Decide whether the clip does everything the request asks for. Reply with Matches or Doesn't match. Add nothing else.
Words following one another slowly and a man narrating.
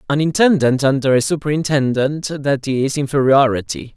Matches